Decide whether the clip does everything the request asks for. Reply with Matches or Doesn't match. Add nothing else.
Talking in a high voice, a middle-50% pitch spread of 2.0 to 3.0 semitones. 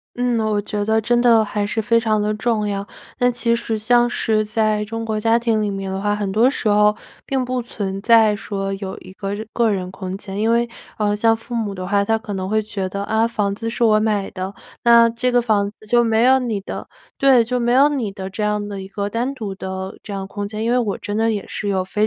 Matches